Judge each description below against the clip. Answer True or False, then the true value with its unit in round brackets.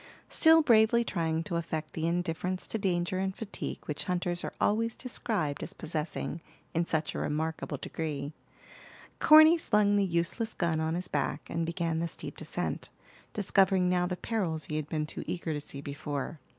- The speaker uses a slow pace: False (175 wpm)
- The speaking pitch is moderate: True (170 Hz)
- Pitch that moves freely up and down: False (3.8 semitones)